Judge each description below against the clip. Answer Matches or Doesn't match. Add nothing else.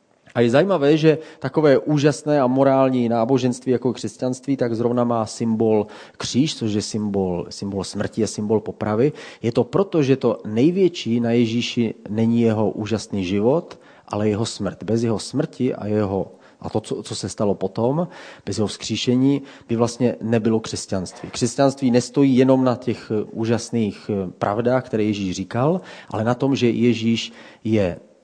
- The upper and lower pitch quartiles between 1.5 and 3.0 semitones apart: Doesn't match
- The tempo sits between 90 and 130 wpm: Doesn't match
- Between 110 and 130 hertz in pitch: Matches